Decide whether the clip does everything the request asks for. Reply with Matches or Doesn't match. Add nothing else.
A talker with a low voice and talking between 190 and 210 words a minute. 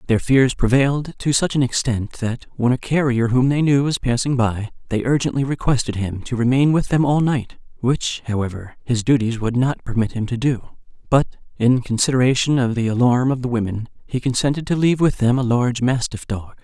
Matches